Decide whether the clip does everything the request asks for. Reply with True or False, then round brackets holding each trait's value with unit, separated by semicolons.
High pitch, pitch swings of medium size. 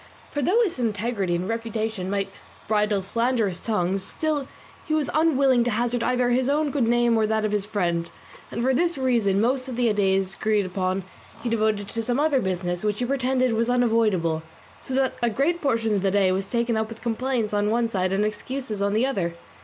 True (225 Hz; 3.9 semitones)